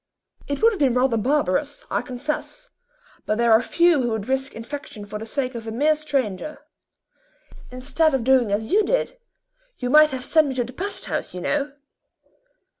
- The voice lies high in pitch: Yes, very high, 265 Hz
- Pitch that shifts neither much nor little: Yes, average, 4.5 semitones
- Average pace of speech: Yes, average, 190 wpm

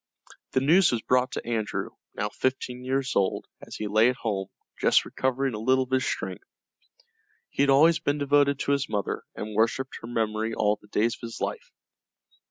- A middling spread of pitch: Yes, average, 3.7 semitones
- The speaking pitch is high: No, low, 125 Hz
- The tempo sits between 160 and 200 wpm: Yes, average, 190 wpm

